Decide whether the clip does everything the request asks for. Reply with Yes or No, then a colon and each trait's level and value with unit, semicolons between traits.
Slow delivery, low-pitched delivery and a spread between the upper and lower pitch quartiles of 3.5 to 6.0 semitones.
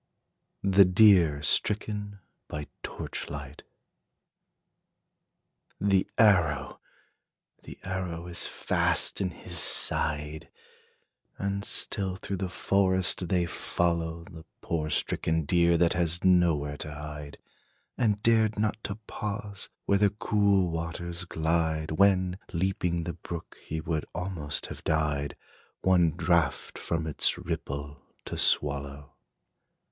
Yes: slow, 115 wpm; very low, 85 Hz; average, 3.8 semitones